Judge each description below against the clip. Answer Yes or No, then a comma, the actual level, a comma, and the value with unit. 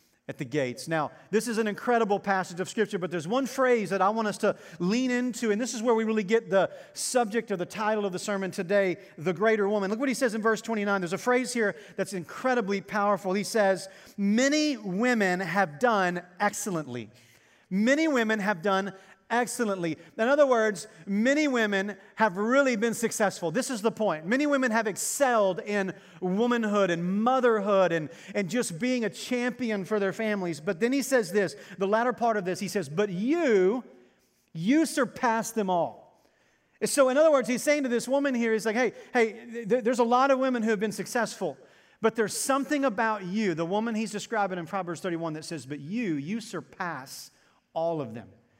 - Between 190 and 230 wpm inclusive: Yes, average, 200 wpm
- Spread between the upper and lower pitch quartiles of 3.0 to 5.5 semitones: Yes, average, 4.0 semitones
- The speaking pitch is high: Yes, high, 210 Hz